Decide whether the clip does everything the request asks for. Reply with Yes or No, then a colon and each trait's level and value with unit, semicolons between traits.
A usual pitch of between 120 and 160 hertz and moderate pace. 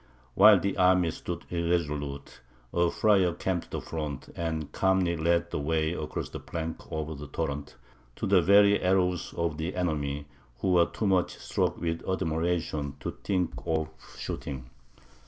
No: very low, 85 Hz; average, 155 wpm